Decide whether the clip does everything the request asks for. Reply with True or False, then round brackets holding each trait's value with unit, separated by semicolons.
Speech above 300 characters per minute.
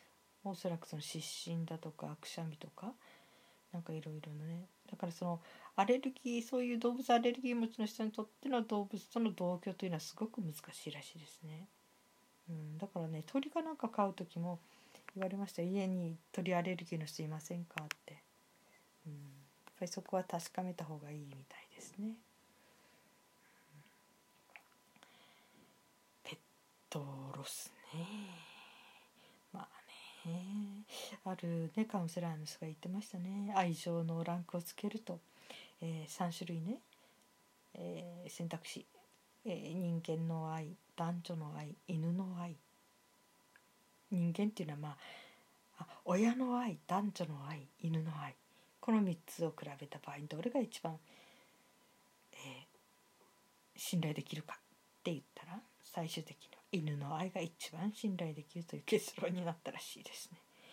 False (280 characters per minute)